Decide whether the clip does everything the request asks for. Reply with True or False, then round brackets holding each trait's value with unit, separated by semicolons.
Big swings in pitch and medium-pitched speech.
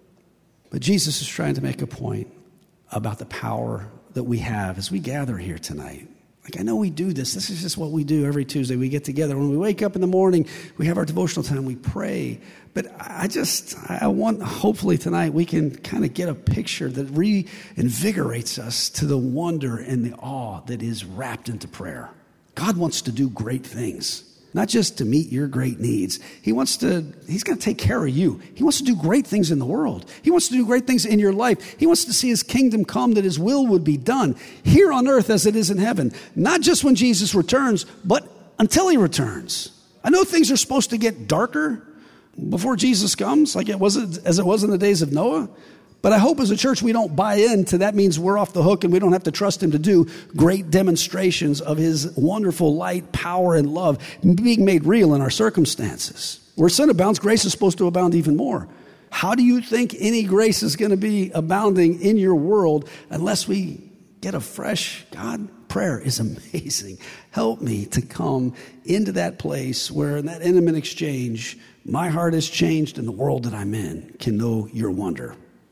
True (7.0 semitones; 175 Hz)